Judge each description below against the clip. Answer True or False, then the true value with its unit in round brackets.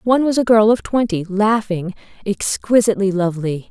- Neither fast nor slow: True (145 wpm)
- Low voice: False (205 Hz)